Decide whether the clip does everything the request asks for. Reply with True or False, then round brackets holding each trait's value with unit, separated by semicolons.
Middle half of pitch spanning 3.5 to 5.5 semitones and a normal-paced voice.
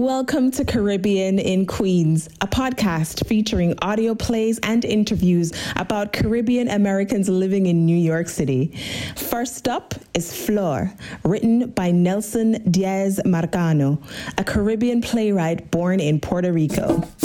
False (4.7 semitones; 125 wpm)